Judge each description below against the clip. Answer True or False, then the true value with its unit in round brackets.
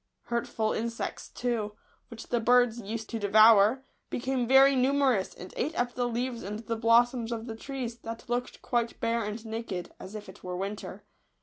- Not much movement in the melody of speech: True (2.0 semitones)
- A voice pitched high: True (230 Hz)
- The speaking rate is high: False (185 wpm)